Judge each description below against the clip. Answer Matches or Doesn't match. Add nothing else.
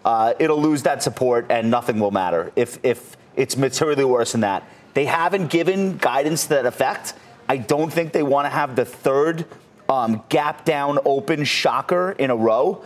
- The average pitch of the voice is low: Doesn't match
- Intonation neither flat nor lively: Matches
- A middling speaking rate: Matches